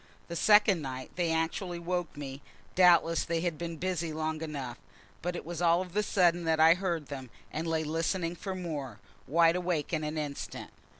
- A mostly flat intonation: Yes, narrow, 2.2 semitones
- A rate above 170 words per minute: Yes, average, 190 wpm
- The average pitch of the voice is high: No, medium, 165 Hz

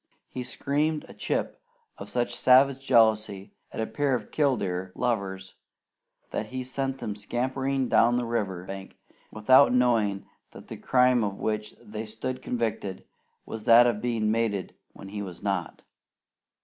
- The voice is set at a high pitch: No, low, 115 Hz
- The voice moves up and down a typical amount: Yes, average, 3.6 semitones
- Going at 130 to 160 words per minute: Yes, average, 150 wpm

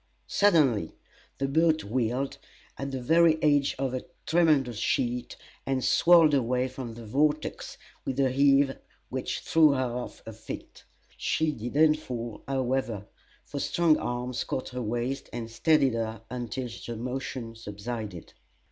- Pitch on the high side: No, low, 130 Hz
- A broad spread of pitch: No, average, 3.3 semitones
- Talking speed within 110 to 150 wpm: Yes, average, 145 wpm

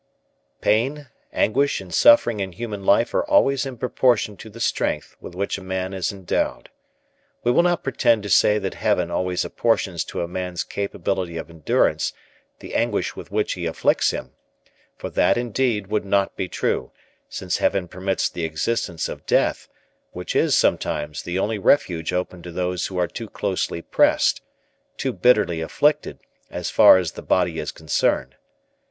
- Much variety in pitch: No, average, 4.6 semitones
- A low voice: Yes, very low, 95 Hz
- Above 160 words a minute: Yes, average, 170 wpm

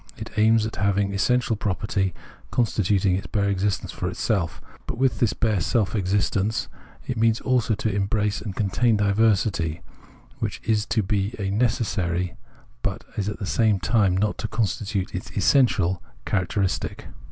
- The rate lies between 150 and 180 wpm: Yes, average, 155 wpm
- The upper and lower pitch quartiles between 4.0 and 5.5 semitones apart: No, narrow, 2.5 semitones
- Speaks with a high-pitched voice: No, low, 105 Hz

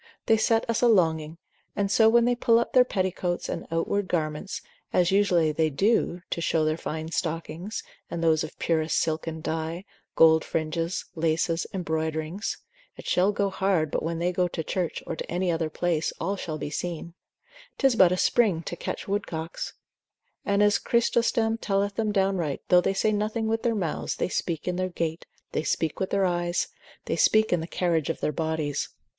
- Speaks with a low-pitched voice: No, medium, 175 Hz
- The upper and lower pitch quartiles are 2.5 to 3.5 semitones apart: No, average, 4.0 semitones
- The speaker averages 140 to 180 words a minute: No, average, 190 wpm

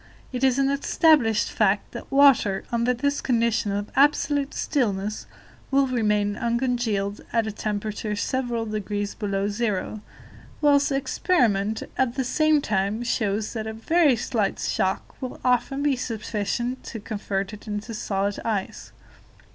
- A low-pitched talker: No, high, 225 Hz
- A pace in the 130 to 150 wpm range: Yes, average, 140 wpm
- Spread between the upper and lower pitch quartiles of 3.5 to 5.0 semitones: Yes, average, 4.1 semitones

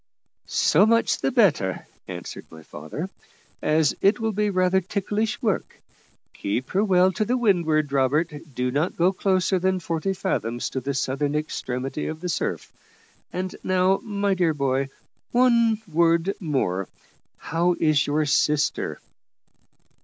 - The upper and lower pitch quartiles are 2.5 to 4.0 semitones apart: No, average, 5.2 semitones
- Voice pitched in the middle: Yes, medium, 170 Hz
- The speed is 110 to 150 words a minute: Yes, average, 140 wpm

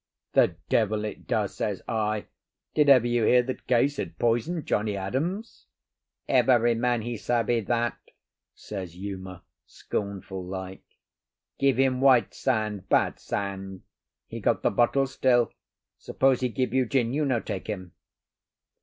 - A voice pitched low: Yes, low, 115 Hz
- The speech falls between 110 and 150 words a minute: Yes, average, 140 wpm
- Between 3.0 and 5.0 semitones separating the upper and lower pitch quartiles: Yes, average, 4.1 semitones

